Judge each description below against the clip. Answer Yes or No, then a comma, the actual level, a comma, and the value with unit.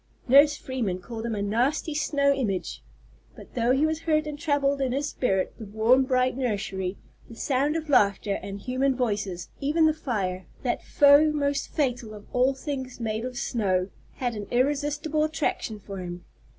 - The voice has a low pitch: No, very high, 255 Hz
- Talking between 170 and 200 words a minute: Yes, average, 175 wpm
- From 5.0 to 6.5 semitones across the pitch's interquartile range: Yes, average, 5.3 semitones